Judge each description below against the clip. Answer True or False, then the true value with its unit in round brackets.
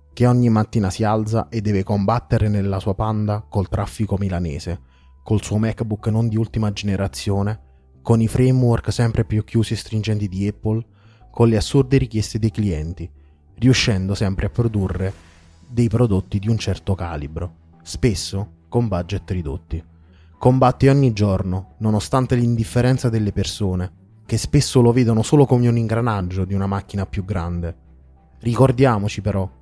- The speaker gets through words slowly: False (150 wpm)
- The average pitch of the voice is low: True (105 Hz)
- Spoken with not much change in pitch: False (3.5 semitones)